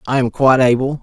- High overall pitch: No, low, 130 Hz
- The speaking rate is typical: No, fast, 235 wpm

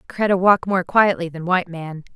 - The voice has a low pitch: No, medium, 180 Hz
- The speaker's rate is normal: Yes, average, 195 wpm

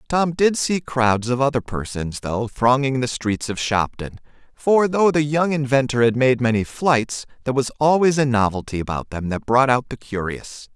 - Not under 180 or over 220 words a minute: Yes, average, 190 wpm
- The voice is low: Yes, low, 130 Hz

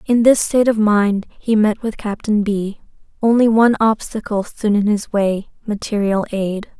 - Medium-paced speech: Yes, average, 160 wpm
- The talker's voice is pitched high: Yes, high, 210 Hz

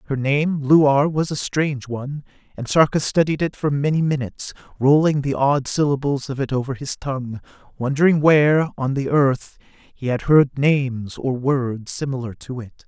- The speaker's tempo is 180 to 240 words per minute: No, average, 170 wpm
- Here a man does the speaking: Yes, male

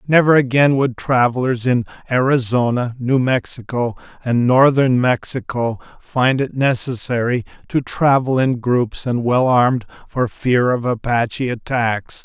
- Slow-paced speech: Yes, slow, 125 wpm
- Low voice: Yes, low, 125 Hz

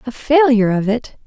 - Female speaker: Yes, female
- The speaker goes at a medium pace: Yes, average, 190 wpm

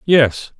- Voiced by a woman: No, male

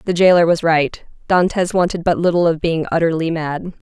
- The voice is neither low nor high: Yes, medium, 165 Hz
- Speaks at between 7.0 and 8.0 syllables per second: No, 5.4 syllables/s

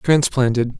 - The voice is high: No, low, 130 Hz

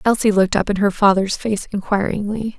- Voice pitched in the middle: No, high, 205 Hz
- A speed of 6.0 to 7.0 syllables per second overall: No, 5.7 syllables/s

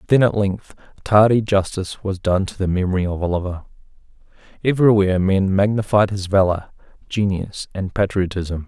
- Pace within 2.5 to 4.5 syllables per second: No, 5.4 syllables/s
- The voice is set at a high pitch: No, very low, 95 Hz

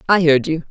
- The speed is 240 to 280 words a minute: Yes, fast, 255 wpm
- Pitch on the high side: No, medium, 175 Hz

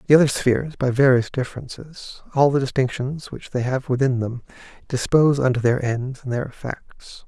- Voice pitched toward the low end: Yes, low, 130 Hz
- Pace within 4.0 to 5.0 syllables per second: No, 5.3 syllables/s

